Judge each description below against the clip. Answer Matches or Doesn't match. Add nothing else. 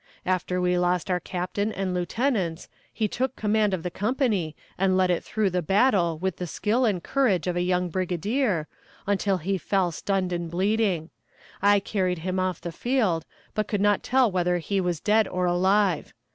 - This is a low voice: Doesn't match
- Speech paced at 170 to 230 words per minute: Matches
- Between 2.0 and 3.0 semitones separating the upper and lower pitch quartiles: Matches